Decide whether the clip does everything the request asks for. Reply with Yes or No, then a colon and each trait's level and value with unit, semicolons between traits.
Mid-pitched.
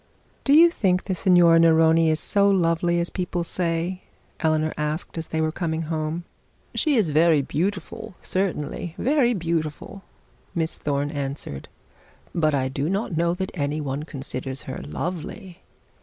Yes: medium, 165 Hz